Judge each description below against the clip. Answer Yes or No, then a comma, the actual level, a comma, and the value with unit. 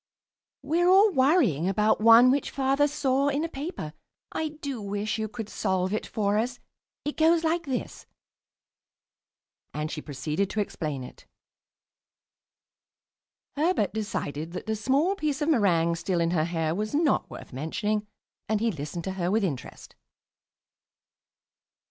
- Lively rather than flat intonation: Yes, wide, 8.4 semitones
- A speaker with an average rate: Yes, average, 145 wpm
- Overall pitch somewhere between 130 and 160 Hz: No, high, 215 Hz